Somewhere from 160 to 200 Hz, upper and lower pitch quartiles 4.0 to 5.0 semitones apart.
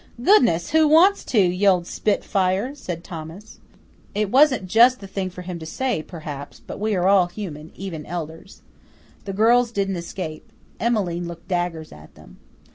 Yes: medium, 185 Hz; average, 4.3 semitones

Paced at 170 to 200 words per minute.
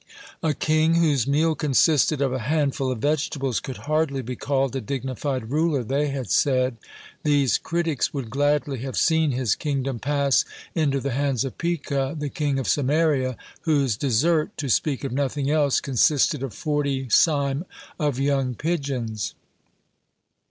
No: average, 150 wpm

